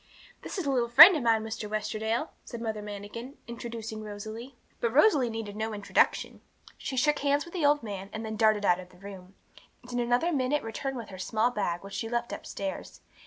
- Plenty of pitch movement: No, average, 3.1 semitones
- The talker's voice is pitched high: Yes, high, 225 Hz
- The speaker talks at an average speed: No, fast, 215 wpm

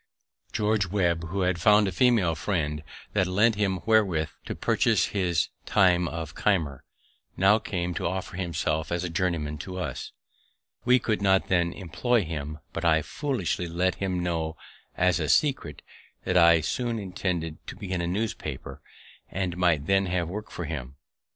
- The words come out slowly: No, average, 165 wpm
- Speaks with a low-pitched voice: Yes, very low, 90 Hz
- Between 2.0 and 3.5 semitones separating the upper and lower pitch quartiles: Yes, average, 3.2 semitones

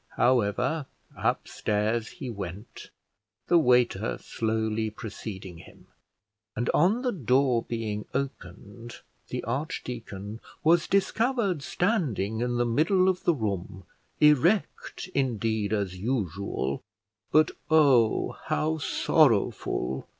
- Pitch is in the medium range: No, low, 120 Hz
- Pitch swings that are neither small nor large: No, wide, 6.5 semitones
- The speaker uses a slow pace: Yes, slow, 100 wpm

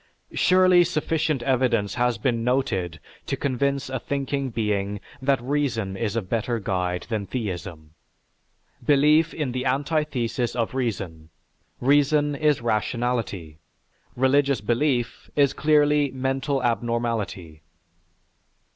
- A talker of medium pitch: No, low, 125 Hz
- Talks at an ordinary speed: No, slow, 110 wpm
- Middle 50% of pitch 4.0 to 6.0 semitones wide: Yes, average, 4.5 semitones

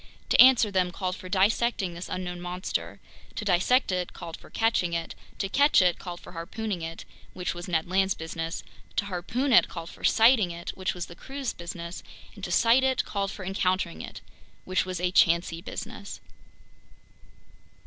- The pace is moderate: Yes, average, 170 wpm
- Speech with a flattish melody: No, average, 3.3 semitones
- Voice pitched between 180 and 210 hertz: Yes, medium, 185 Hz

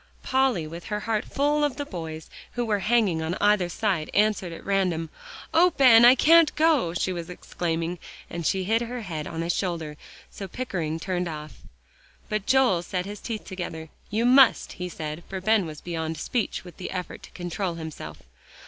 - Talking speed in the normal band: Yes, average, 185 wpm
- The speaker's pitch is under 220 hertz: Yes, medium, 185 Hz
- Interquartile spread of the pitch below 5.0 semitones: No, wide, 5.4 semitones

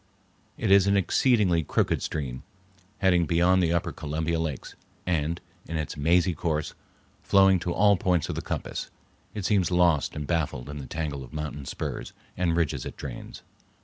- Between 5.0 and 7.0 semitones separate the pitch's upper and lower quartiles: No, average, 3.0 semitones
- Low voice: Yes, very low, 85 Hz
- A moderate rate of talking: Yes, average, 170 wpm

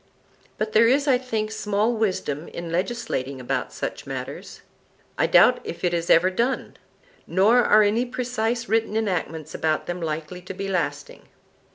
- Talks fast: No, average, 155 wpm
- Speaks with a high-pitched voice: Yes, high, 205 Hz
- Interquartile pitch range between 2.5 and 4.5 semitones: No, average, 5.3 semitones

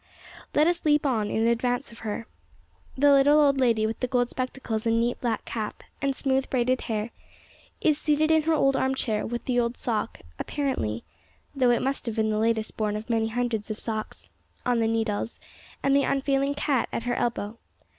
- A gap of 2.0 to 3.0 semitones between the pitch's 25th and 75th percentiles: No, average, 3.5 semitones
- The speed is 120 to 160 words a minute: No, average, 195 wpm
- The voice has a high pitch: Yes, high, 245 Hz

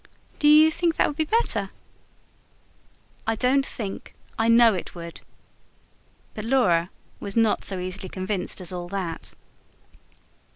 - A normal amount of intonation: No, wide, 6.3 semitones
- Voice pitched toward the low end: No, high, 210 Hz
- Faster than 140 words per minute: No, slow, 135 wpm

